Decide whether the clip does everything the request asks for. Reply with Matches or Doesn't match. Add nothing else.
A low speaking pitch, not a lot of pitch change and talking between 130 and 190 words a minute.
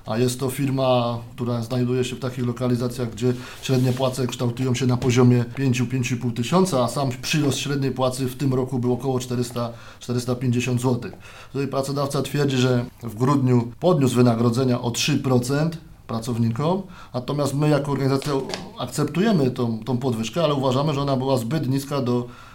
Matches